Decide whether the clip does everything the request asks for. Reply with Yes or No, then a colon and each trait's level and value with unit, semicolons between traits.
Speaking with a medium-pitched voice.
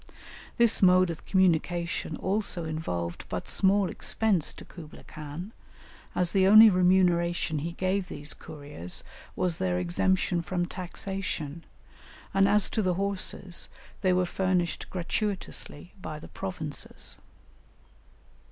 Yes: medium, 180 Hz